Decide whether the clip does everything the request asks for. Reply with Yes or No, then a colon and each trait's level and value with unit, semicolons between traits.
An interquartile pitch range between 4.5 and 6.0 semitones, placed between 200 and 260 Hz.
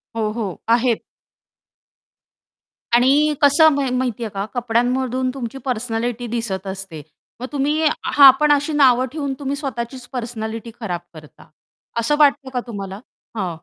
No: average, 3.6 semitones; high, 245 Hz